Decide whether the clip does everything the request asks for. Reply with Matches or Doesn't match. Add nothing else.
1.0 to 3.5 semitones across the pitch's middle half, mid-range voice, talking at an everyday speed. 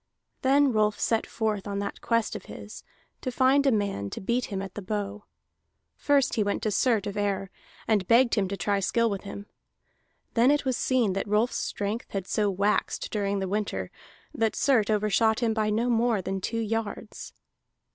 Doesn't match